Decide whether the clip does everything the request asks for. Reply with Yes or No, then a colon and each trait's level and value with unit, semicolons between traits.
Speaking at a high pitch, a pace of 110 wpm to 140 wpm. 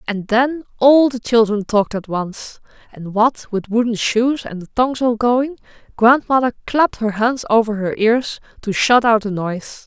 No: high, 230 Hz; average, 185 wpm